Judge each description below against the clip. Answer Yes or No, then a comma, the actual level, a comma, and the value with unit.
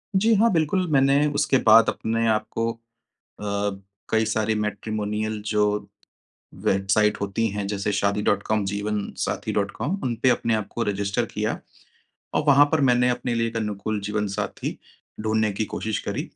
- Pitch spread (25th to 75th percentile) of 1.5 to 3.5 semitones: Yes, narrow, 2.4 semitones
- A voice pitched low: Yes, low, 110 Hz